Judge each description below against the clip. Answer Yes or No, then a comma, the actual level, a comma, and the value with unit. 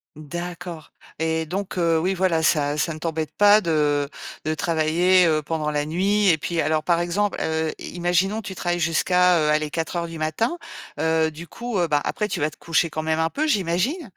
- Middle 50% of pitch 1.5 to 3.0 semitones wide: Yes, narrow, 2.6 semitones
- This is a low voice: No, medium, 165 Hz